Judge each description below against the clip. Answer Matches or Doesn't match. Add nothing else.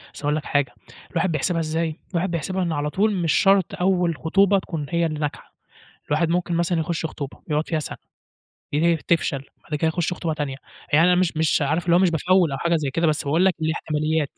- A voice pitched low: Doesn't match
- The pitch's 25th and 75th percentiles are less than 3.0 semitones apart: Matches